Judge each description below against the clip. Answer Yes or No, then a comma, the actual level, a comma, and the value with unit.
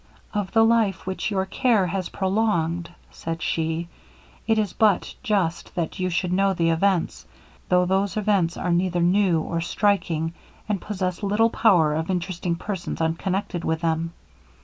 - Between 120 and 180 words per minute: Yes, average, 155 wpm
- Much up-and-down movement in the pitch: No, average, 3.2 semitones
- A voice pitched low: No, medium, 185 Hz